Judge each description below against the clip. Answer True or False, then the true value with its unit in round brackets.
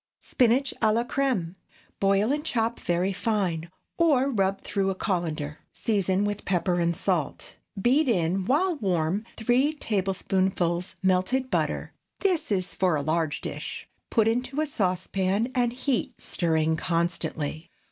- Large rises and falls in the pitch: True (5.8 semitones)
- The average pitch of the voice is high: True (195 Hz)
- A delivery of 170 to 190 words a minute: False (135 wpm)